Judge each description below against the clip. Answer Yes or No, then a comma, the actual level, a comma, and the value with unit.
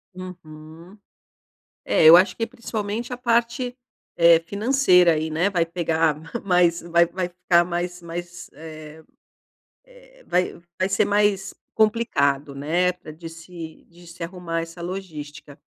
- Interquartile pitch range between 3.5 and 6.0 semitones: No, average, 3.1 semitones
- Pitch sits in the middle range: Yes, medium, 175 Hz